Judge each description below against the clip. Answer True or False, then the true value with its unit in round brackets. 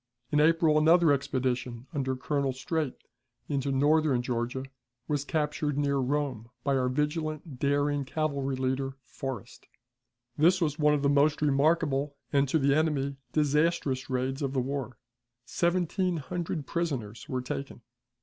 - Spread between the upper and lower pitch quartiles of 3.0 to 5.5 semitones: False (2.6 semitones)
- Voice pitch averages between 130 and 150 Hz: True (140 Hz)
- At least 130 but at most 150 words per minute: True (140 wpm)